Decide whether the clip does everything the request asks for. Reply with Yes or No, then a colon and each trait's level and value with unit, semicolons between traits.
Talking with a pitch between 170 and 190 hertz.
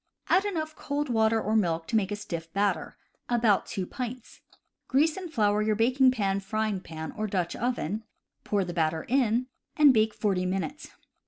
No: high, 215 Hz